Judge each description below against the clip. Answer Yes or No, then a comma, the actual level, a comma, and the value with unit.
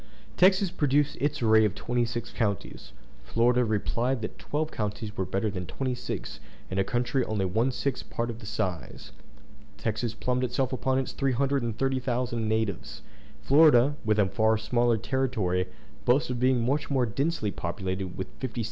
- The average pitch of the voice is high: No, low, 120 Hz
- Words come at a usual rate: Yes, average, 160 wpm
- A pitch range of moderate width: Yes, average, 3.4 semitones